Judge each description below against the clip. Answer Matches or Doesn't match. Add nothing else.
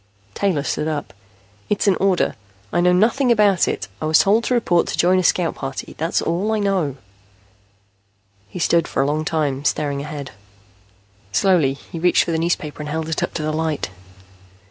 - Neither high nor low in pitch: Matches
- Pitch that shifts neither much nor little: Matches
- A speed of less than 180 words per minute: Doesn't match